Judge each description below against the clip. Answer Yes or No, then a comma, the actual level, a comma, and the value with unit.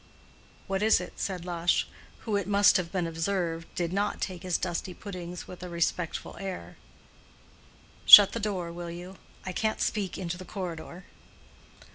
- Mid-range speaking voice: Yes, medium, 180 Hz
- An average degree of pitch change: No, narrow, 2.3 semitones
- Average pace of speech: Yes, average, 160 wpm